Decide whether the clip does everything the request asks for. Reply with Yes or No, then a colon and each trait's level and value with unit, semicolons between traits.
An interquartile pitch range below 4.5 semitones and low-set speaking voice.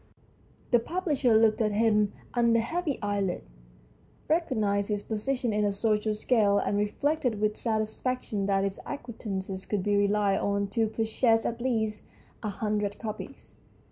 No: narrow, 2.5 semitones; high, 215 Hz